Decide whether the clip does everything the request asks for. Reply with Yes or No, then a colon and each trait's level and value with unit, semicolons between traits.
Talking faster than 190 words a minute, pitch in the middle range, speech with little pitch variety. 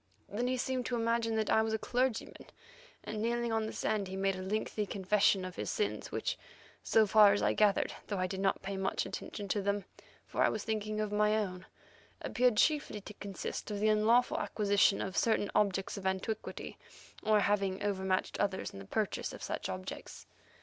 No: average, 200 wpm; high, 210 Hz; narrow, 2.1 semitones